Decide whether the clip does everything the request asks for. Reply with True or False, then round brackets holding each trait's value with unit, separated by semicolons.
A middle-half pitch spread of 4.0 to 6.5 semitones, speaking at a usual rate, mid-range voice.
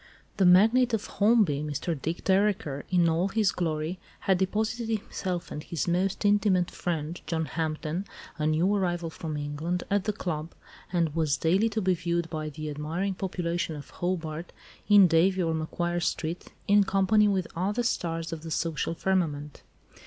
False (3.4 semitones; 165 wpm; 175 Hz)